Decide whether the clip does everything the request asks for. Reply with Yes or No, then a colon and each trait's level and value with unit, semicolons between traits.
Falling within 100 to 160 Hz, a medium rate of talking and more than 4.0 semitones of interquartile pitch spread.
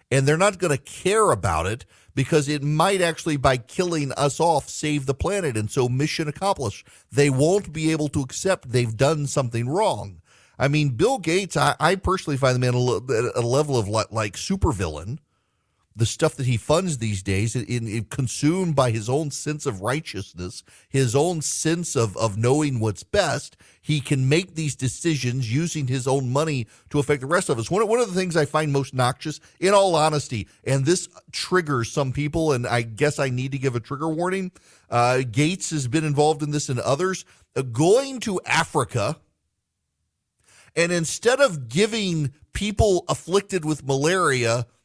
Yes: medium, 140 Hz; average, 180 wpm; average, 4.9 semitones